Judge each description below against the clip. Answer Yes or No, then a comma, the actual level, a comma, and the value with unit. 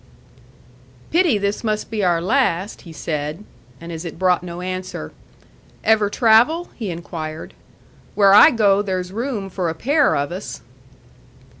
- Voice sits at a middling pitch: No, high, 195 Hz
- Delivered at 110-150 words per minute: Yes, average, 145 wpm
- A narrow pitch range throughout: No, average, 4.3 semitones